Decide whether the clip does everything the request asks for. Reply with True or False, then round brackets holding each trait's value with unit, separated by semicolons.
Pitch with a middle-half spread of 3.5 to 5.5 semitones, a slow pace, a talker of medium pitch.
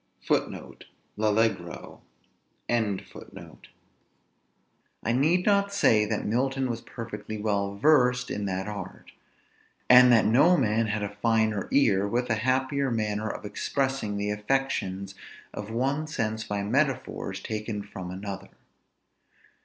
False (4.2 semitones; 115 wpm; 110 Hz)